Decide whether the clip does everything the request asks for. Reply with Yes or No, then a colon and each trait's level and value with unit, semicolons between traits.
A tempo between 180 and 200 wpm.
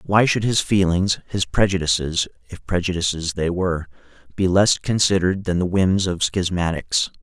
No: average, 150 wpm